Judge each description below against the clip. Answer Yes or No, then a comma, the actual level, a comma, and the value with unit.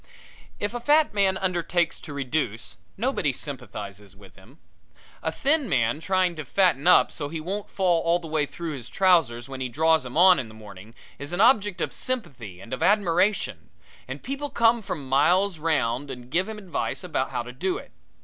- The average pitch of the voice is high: No, medium, 165 Hz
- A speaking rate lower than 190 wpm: No, average, 195 wpm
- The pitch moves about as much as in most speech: No, wide, 7.0 semitones